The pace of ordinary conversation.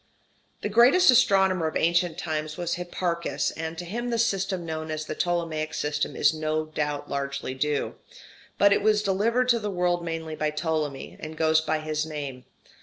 Yes: average, 180 wpm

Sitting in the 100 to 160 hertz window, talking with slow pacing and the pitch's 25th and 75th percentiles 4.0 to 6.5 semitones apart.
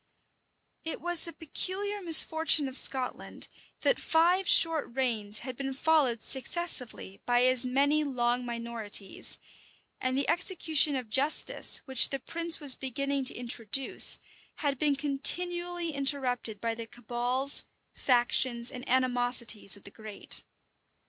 No: very high, 265 Hz; slow, 130 wpm; average, 4.4 semitones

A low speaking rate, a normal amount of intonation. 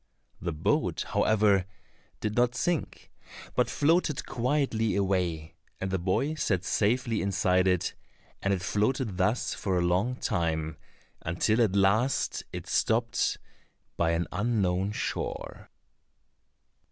Yes: slow, 120 wpm; average, 4.6 semitones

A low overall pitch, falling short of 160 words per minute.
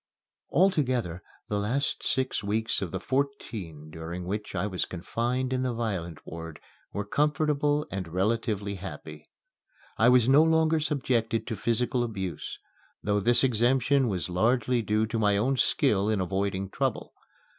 Yes: low, 110 Hz; average, 145 wpm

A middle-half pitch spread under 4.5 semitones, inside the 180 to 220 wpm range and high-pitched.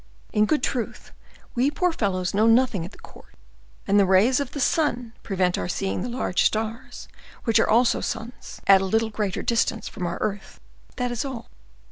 Yes: average, 4.0 semitones; average, 185 wpm; high, 225 Hz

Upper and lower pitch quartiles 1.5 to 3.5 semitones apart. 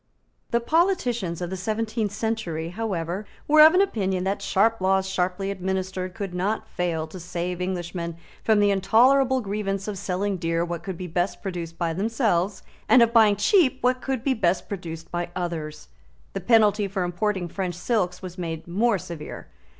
No: average, 3.9 semitones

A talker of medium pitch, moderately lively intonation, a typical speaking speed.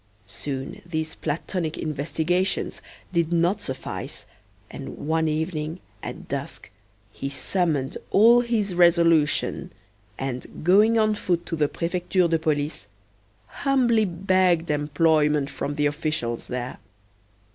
No: medium, 165 Hz; average, 3.7 semitones; slow, 115 wpm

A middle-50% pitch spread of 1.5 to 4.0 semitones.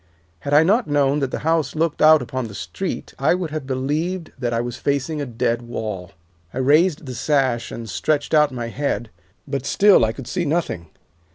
No: average, 4.4 semitones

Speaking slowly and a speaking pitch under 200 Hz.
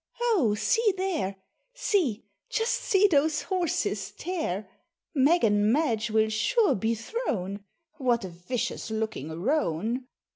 No: slow, 120 wpm; high, 245 Hz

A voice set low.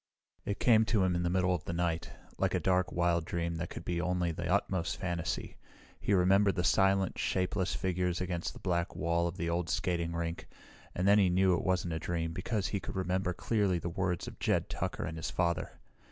Yes: very low, 90 Hz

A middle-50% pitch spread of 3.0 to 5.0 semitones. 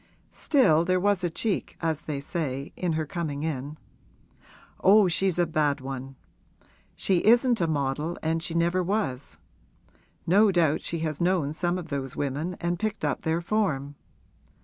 Yes: average, 3.9 semitones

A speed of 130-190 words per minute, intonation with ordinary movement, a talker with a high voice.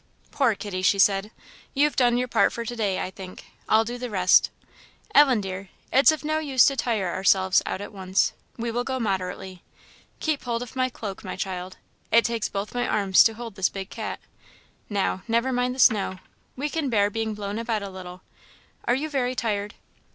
No: fast, 205 wpm; average, 4.2 semitones; high, 220 Hz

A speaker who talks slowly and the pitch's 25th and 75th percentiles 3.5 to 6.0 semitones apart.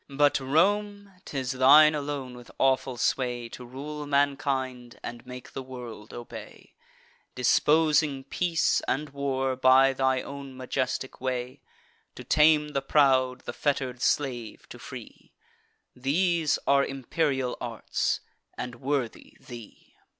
No: slow, 120 wpm; narrow, 2.4 semitones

